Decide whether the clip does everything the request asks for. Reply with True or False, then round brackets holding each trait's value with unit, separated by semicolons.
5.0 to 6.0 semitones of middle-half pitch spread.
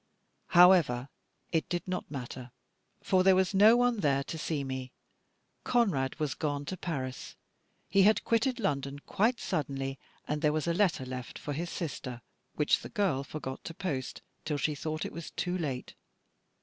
True (5.3 semitones)